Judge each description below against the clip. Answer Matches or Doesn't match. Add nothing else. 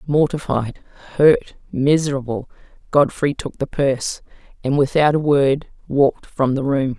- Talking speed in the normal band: Doesn't match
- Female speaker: Matches